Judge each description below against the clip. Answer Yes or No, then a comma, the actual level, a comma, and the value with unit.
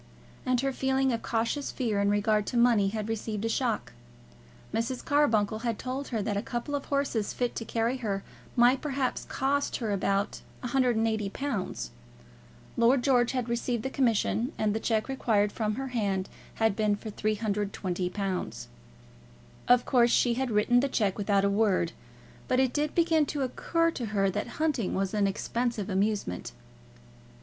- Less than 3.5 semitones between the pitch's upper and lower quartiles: No, average, 3.8 semitones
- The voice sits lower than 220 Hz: No, high, 230 Hz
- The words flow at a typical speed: Yes, average, 160 wpm